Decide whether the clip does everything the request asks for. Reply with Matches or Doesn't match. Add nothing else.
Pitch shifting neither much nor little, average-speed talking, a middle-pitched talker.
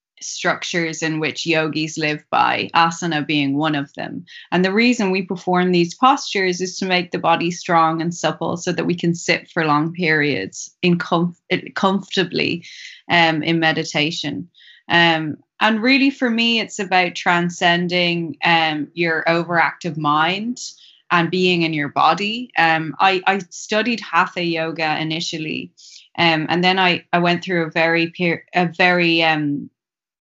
Doesn't match